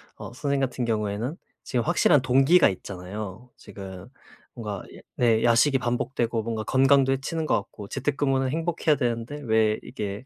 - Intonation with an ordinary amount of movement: Yes, average, 3.9 semitones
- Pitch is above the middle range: No, low, 120 Hz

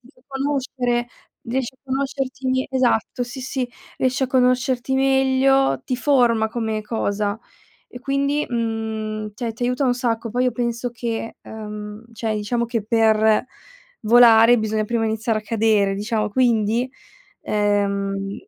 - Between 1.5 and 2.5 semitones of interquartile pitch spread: No, average, 2.9 semitones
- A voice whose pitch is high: Yes, high, 235 Hz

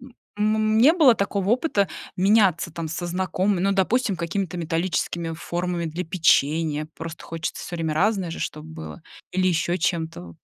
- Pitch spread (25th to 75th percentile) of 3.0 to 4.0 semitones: Yes, average, 3.5 semitones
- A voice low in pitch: No, medium, 175 Hz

